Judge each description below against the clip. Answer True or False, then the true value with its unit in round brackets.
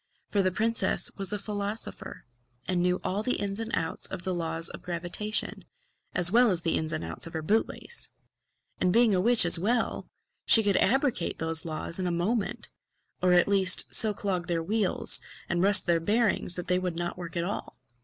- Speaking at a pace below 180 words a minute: False (205 wpm)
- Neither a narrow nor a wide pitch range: True (3.4 semitones)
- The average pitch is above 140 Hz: True (185 Hz)